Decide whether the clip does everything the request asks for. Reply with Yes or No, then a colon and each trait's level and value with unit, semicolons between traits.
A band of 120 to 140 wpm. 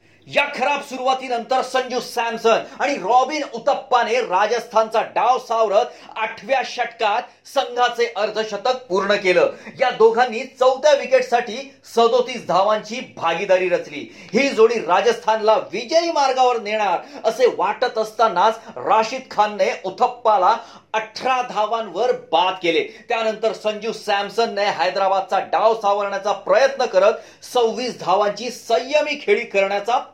No: average, 105 wpm